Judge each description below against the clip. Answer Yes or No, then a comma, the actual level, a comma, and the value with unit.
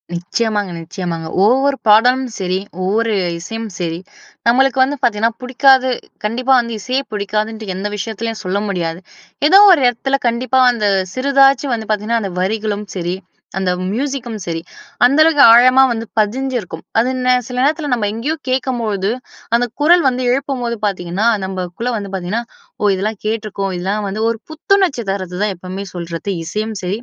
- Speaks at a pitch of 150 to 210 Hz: No, high, 225 Hz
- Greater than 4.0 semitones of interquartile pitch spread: Yes, average, 4.7 semitones